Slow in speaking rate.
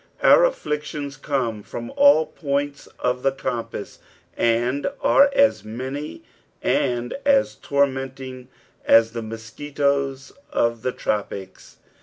Yes: slow, 110 wpm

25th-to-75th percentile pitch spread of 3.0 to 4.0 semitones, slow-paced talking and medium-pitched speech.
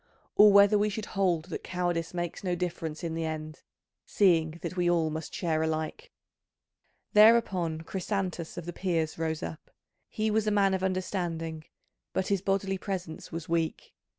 No: average, 3.3 semitones; average, 165 wpm; medium, 175 Hz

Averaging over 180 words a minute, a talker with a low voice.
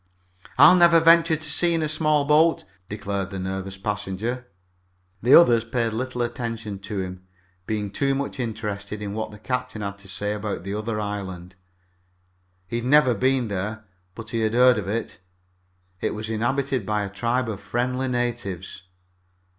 No: average, 170 wpm; low, 115 Hz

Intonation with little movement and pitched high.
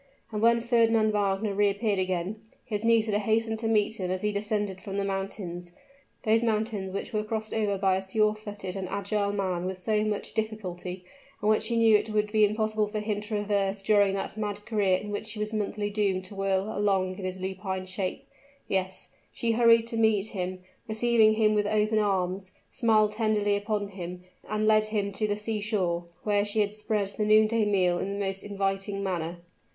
Yes: narrow, 1.9 semitones; high, 205 Hz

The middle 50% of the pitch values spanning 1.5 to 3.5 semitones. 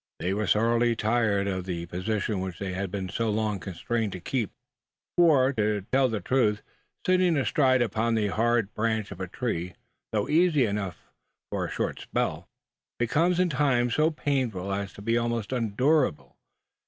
No: average, 4.6 semitones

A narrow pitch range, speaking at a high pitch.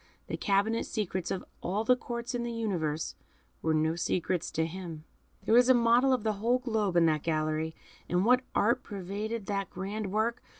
No: average, 5.2 semitones; high, 200 Hz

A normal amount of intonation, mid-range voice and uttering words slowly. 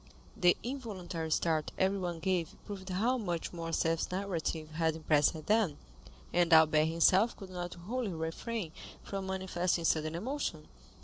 Yes: average, 3.2 semitones; medium, 175 Hz; slow, 130 wpm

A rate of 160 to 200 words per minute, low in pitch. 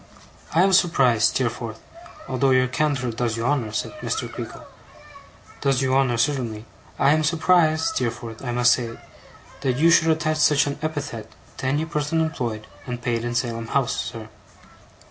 Yes: average, 165 wpm; low, 130 Hz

